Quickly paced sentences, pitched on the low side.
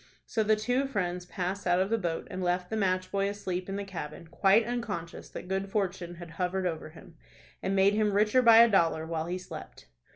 No: fast, 220 wpm; high, 190 Hz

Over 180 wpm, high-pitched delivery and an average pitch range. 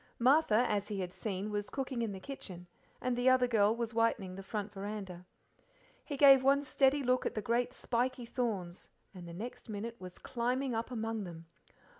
Yes: average, 190 wpm; high, 230 Hz; average, 4.1 semitones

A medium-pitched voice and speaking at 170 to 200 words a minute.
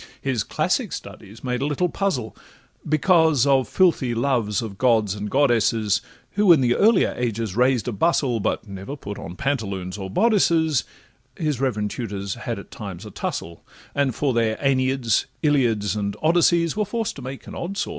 No: low, 125 Hz; average, 175 wpm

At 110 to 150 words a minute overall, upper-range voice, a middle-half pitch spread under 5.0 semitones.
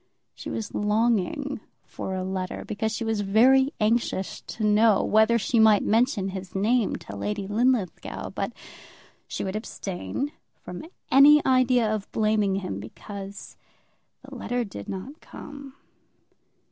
Yes: slow, 135 wpm; high, 215 Hz; average, 3.8 semitones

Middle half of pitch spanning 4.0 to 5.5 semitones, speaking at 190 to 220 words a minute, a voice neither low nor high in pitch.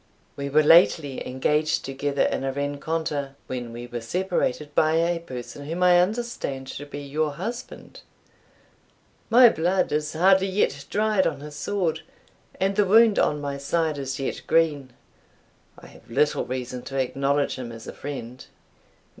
No: average, 4.4 semitones; average, 155 wpm; medium, 150 Hz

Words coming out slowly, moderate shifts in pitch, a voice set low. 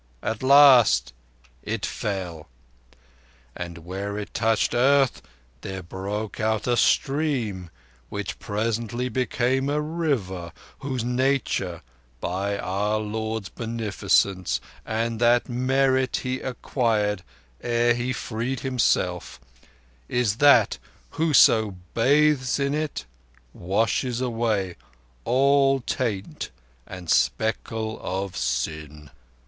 Yes: slow, 100 wpm; average, 4.6 semitones; low, 115 Hz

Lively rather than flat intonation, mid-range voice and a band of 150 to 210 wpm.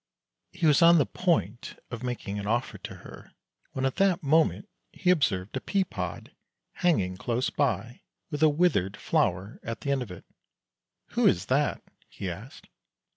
No: wide, 7.7 semitones; low, 125 Hz; average, 180 wpm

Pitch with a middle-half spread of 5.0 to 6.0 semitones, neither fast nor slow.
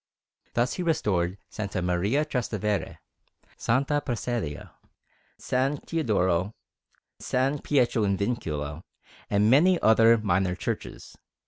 No: wide, 5.6 semitones; slow, 100 wpm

